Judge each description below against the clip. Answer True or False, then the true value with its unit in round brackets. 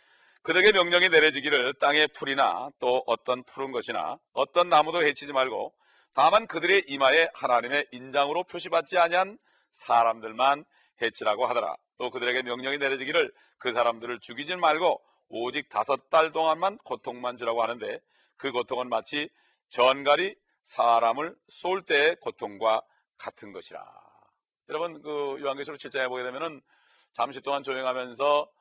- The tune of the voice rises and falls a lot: False (5.0 semitones)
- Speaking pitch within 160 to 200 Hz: False (140 Hz)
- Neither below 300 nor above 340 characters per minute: True (330 characters per minute)